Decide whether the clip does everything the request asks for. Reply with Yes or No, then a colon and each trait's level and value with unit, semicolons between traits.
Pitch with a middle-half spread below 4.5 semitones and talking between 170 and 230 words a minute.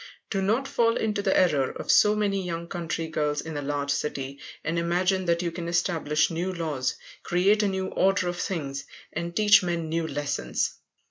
Yes: average, 3.9 semitones; average, 185 wpm